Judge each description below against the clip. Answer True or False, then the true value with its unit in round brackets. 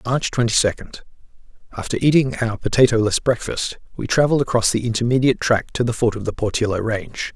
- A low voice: True (115 Hz)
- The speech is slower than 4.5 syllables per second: False (6.1 syllables/s)